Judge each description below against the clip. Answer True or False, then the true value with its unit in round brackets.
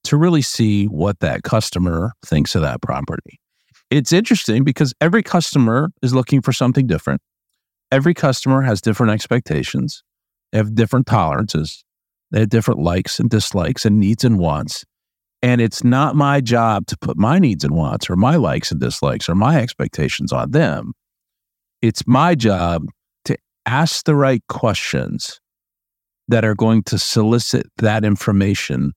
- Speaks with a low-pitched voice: True (115 Hz)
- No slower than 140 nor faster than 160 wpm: True (155 wpm)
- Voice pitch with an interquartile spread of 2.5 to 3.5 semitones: False (4.1 semitones)